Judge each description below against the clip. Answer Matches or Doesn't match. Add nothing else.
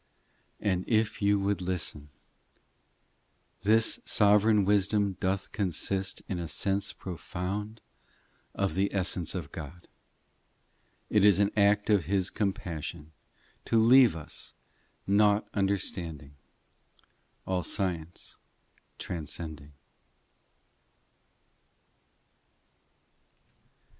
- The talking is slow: Matches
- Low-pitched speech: Matches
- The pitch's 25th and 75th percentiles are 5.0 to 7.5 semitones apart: Doesn't match